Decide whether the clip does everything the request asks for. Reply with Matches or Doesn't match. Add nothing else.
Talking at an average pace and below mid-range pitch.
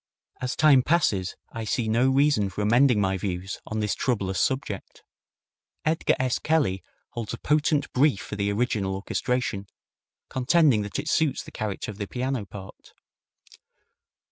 Matches